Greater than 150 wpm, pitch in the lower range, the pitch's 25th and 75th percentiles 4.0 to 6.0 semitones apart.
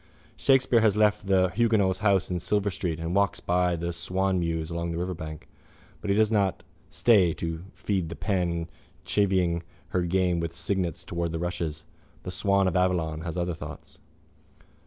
No: average, 165 wpm; very low, 90 Hz; average, 2.8 semitones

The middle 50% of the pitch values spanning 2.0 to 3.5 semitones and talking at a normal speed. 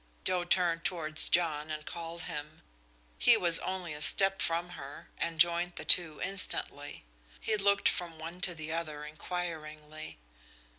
Yes: narrow, 2.4 semitones; average, 150 wpm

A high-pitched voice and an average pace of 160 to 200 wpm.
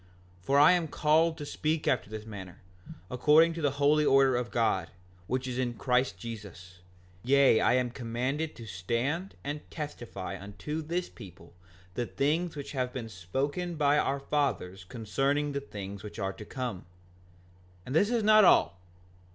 No: low, 130 Hz; average, 170 wpm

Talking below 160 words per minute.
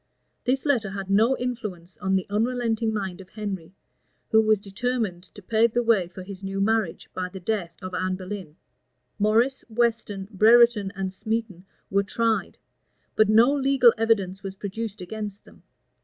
No: average, 165 wpm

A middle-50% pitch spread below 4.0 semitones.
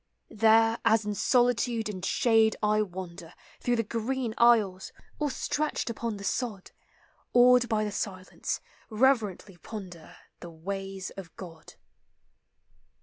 Yes: average, 3.6 semitones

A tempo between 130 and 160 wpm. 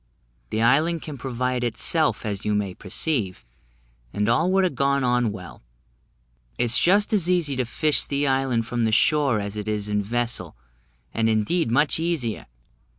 No: average, 170 wpm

